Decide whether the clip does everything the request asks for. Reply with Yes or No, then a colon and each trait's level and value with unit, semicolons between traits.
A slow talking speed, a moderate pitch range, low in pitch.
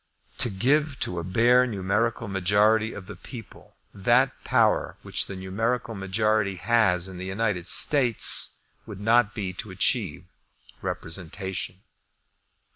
Yes: slow, 125 wpm; average, 3.6 semitones; low, 105 Hz